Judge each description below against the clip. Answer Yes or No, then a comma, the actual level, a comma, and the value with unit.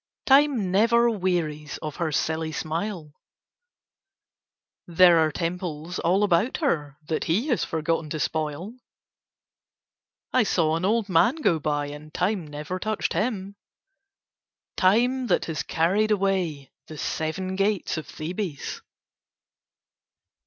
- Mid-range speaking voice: Yes, medium, 175 Hz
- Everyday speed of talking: No, slow, 120 wpm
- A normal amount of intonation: Yes, average, 4.9 semitones